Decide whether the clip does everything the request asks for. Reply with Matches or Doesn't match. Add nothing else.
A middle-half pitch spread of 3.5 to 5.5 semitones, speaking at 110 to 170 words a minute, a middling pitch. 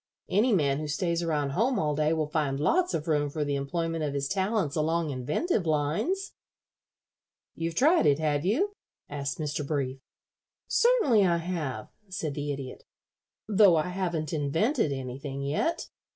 Matches